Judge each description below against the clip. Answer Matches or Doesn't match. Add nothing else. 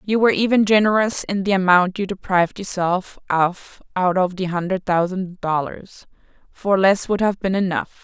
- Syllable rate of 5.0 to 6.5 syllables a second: Doesn't match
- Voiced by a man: Doesn't match